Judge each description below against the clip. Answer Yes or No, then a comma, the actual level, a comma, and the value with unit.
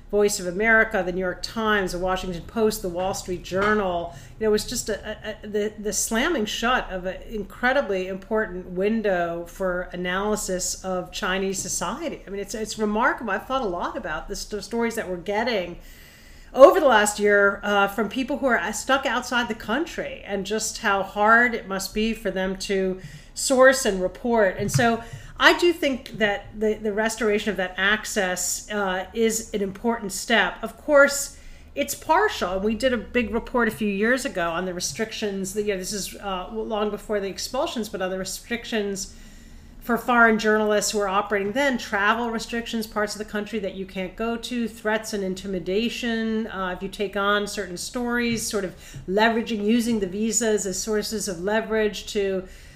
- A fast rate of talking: No, average, 185 wpm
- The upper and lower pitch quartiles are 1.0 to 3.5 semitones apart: Yes, average, 3.0 semitones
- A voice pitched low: No, high, 210 Hz